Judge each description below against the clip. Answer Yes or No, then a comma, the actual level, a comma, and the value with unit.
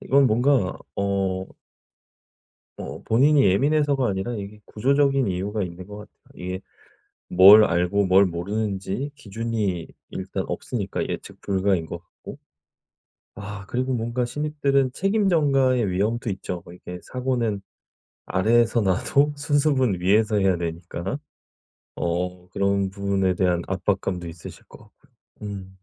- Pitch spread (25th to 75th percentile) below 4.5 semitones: No, average, 5.2 semitones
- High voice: No, low, 100 Hz